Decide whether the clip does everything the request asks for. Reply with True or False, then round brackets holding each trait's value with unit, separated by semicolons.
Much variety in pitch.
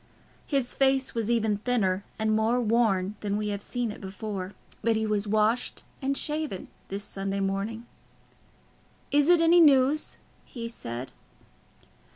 False (3.8 semitones)